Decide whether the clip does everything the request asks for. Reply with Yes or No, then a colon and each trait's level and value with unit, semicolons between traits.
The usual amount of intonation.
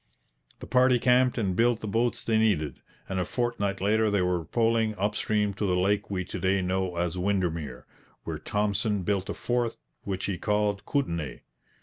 Yes: average, 3.3 semitones